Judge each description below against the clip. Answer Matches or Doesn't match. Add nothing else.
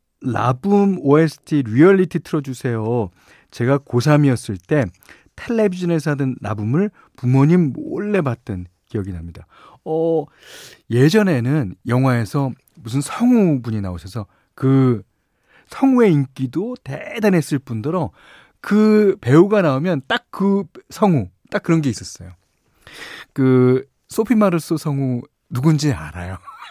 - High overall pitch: Doesn't match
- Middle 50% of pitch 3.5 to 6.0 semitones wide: Doesn't match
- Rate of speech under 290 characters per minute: Matches